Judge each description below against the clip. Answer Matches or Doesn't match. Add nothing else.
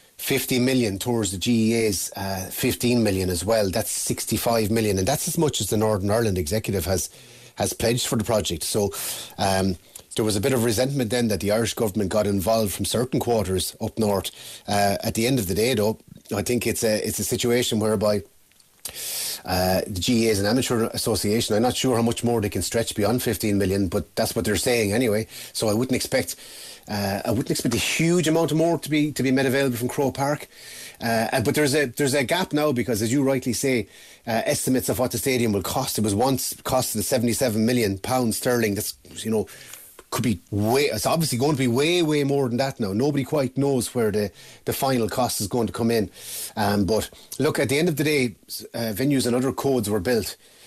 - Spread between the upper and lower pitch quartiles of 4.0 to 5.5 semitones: Doesn't match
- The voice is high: Doesn't match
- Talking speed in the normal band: Doesn't match